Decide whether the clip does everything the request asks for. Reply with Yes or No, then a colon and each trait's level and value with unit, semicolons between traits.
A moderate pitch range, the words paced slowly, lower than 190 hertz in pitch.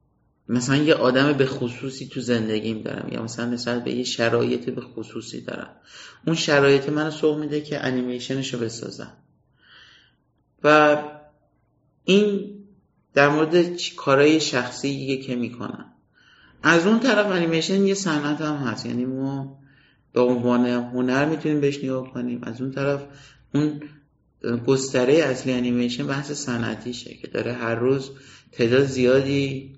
No: average, 3.2 semitones; average, 135 wpm; low, 135 Hz